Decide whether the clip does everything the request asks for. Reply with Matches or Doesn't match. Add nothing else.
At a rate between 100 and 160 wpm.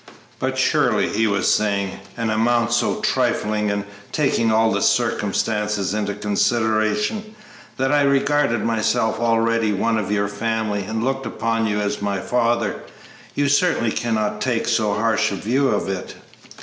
Matches